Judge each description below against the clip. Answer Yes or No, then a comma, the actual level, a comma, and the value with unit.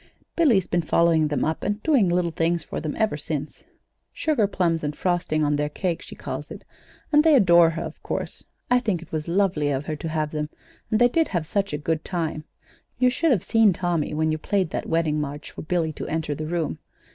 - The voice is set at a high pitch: No, medium, 165 Hz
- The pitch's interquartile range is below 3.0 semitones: No, average, 4.3 semitones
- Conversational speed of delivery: No, fast, 220 wpm